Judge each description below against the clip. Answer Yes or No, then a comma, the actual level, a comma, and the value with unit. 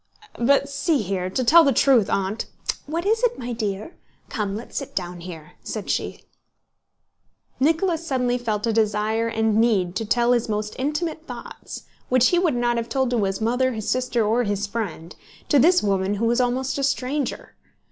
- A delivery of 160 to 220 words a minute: Yes, average, 185 wpm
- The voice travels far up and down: No, average, 4.5 semitones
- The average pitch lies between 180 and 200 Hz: No, high, 235 Hz